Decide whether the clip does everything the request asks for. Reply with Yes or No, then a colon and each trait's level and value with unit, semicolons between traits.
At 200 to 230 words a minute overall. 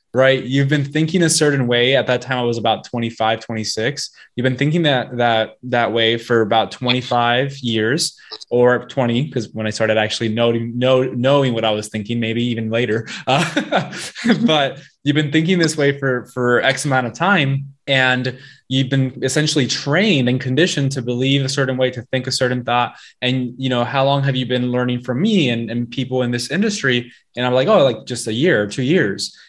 Yes: fast, 205 wpm